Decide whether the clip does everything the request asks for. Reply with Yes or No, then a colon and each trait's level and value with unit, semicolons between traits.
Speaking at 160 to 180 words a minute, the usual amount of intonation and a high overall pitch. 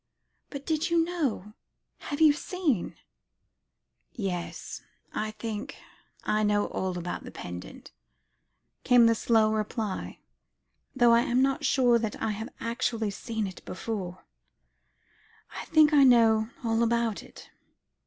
No: slow, 135 wpm; average, 3.8 semitones; high, 230 Hz